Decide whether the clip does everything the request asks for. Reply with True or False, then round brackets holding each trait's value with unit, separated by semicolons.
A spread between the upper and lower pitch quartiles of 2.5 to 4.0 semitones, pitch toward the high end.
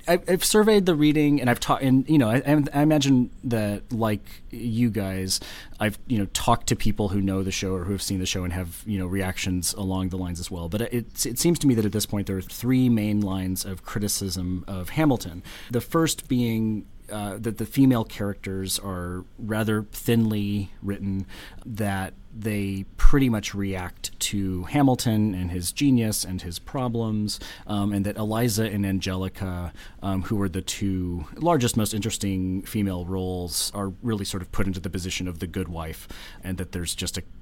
False (3.5 semitones; 100 Hz)